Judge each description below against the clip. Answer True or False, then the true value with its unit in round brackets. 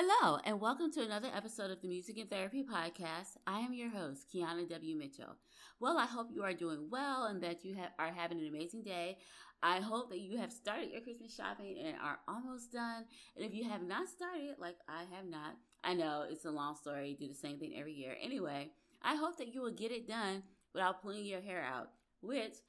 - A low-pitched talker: False (195 Hz)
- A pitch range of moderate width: False (6.0 semitones)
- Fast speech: True (225 wpm)